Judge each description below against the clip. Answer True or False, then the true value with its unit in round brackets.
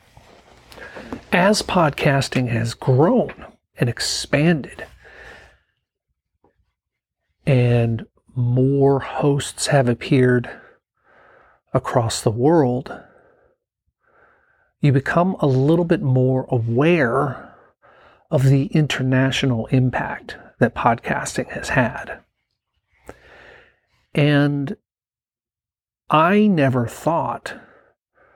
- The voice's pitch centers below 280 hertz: True (140 Hz)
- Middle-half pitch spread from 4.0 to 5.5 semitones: True (4.4 semitones)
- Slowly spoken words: True (70 wpm)